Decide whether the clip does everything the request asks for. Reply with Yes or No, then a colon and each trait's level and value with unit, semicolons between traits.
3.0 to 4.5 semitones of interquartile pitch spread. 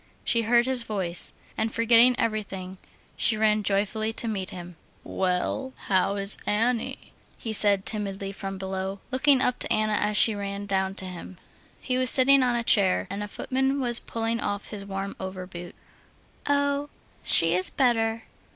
Yes: average, 3.5 semitones